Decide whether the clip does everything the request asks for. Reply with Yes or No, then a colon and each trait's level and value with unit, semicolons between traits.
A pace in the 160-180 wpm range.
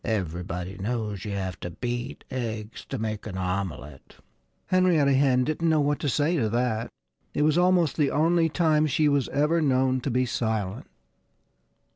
Yes: average, 165 wpm